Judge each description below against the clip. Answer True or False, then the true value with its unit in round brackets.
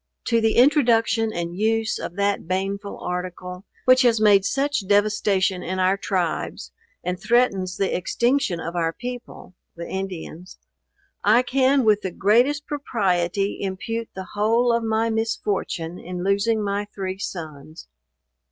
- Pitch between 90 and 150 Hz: False (200 Hz)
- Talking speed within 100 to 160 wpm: True (140 wpm)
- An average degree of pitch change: True (3.8 semitones)